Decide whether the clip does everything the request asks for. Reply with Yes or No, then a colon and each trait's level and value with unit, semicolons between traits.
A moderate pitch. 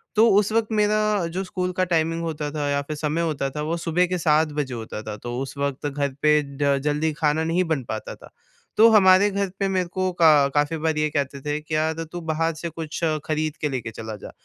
Yes: medium, 155 Hz